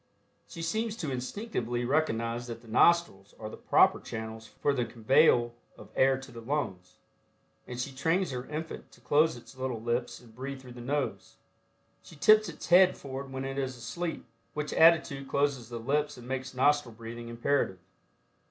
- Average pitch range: Yes, average, 3.9 semitones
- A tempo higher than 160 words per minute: Yes, average, 175 wpm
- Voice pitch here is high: No, low, 130 Hz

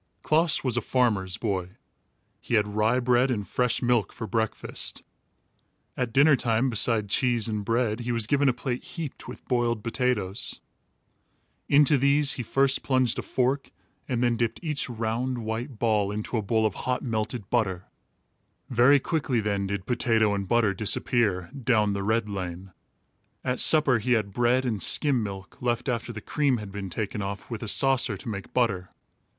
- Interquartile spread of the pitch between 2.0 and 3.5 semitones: Yes, average, 3.2 semitones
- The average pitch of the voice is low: Yes, low, 115 Hz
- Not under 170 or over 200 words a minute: Yes, average, 175 wpm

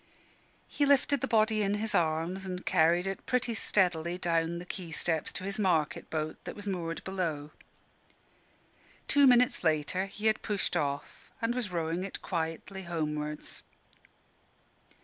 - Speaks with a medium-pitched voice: Yes, medium, 180 Hz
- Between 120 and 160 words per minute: Yes, average, 150 wpm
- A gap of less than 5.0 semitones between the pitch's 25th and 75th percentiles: Yes, average, 4.2 semitones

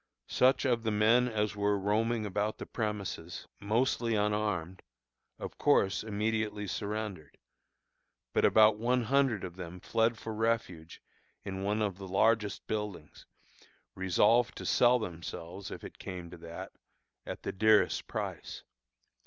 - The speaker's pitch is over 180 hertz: No, low, 105 Hz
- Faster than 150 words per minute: No, slow, 135 wpm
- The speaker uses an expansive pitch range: No, average, 2.8 semitones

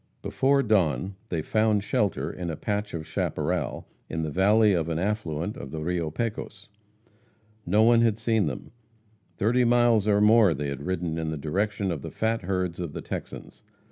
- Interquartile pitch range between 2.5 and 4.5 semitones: No, average, 5.0 semitones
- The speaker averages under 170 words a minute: No, average, 180 wpm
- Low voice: Yes, low, 100 Hz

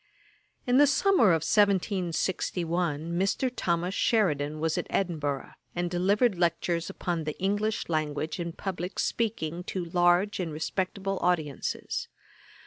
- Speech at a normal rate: No, slow, 125 wpm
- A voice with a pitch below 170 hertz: No, medium, 175 Hz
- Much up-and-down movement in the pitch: No, average, 3.3 semitones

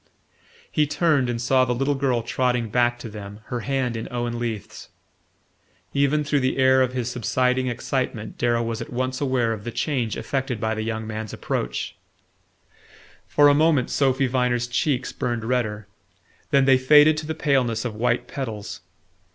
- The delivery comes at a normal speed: Yes, average, 170 wpm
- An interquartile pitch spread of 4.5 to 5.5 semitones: No, narrow, 2.5 semitones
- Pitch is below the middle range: Yes, low, 125 Hz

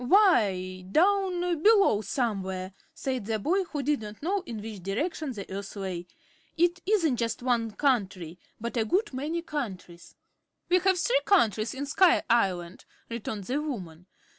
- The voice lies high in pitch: Yes, high, 240 Hz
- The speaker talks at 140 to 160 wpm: Yes, average, 155 wpm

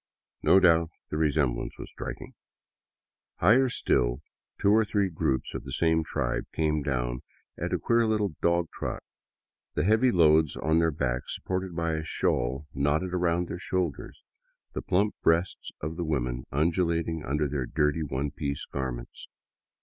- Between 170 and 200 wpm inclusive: No, average, 155 wpm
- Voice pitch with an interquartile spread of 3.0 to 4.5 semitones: Yes, average, 4.1 semitones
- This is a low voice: Yes, very low, 80 Hz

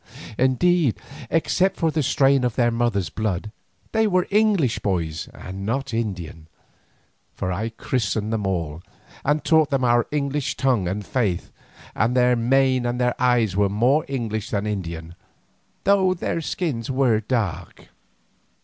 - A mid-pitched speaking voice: No, low, 120 Hz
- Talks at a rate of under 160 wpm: Yes, average, 140 wpm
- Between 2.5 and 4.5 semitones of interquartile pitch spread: No, average, 5.2 semitones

